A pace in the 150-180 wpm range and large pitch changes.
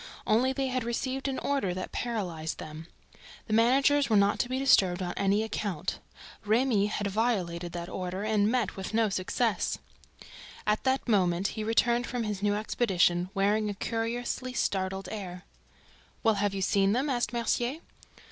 No: average, 165 wpm; average, 4.0 semitones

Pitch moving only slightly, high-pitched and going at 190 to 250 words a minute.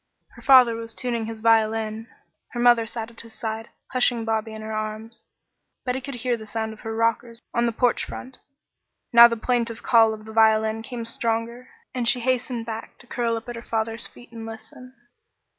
Yes: narrow, 1.4 semitones; high, 230 Hz; average, 195 wpm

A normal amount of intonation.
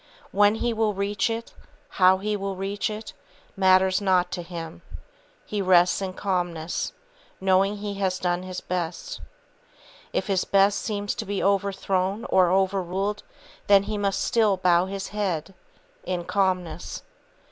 No: narrow, 1.8 semitones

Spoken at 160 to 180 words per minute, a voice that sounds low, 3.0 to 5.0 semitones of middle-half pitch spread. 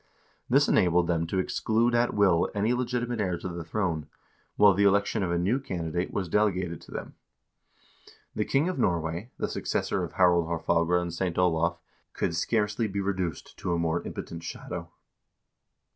Yes: average, 175 wpm; very low, 90 Hz; average, 3.6 semitones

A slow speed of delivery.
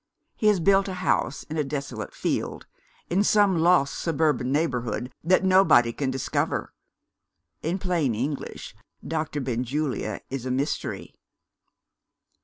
Yes: slow, 125 wpm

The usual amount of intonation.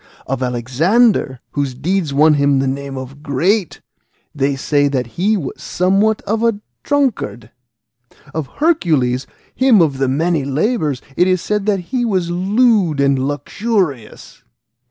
No: wide, 7.0 semitones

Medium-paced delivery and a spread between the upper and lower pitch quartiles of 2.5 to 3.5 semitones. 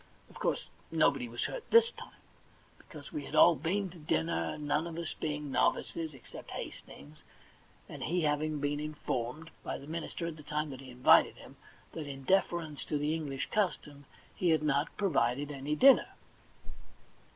Yes: average, 175 wpm; average, 2.9 semitones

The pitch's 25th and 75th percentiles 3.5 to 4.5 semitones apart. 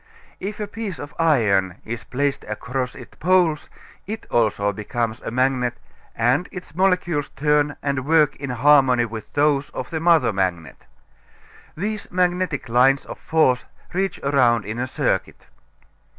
No: wide, 5.6 semitones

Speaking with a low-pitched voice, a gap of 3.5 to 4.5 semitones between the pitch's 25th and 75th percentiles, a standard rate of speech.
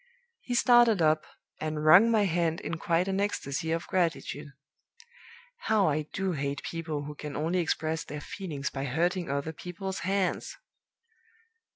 No: medium, 165 Hz; average, 4.0 semitones; average, 150 wpm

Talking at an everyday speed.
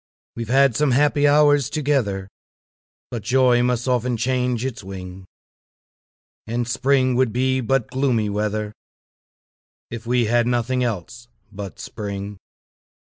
No: slow, 125 wpm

